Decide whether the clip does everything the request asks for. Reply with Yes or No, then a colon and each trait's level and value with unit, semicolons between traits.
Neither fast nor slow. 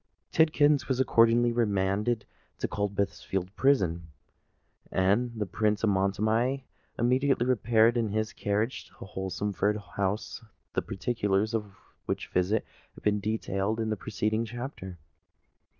No: slow, 120 wpm